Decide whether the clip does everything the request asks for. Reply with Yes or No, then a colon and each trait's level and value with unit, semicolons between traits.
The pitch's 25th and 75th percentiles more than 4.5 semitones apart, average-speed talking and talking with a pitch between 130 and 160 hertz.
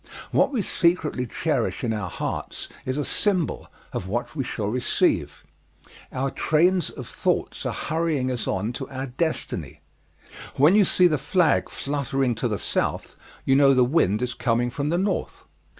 Yes: average, 5.1 semitones; average, 165 wpm; low, 135 Hz